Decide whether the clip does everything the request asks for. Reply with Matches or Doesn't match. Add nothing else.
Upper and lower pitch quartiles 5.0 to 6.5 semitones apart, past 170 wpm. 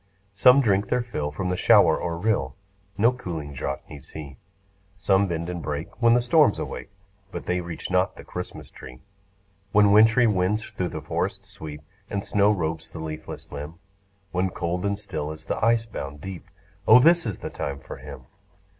Matches